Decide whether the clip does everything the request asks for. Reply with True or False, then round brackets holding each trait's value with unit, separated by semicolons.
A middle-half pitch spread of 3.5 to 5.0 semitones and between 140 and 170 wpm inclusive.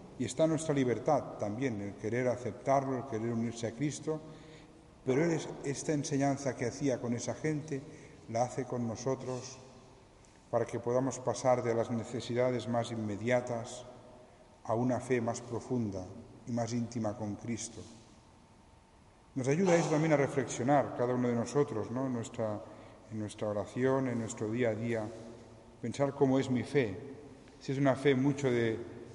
False (3.1 semitones; 160 wpm)